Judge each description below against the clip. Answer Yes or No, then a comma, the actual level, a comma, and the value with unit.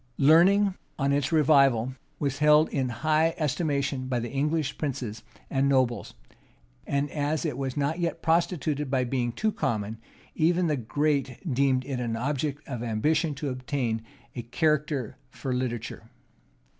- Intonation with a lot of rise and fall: No, average, 3.3 semitones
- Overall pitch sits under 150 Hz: Yes, medium, 140 Hz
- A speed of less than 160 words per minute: Yes, average, 145 wpm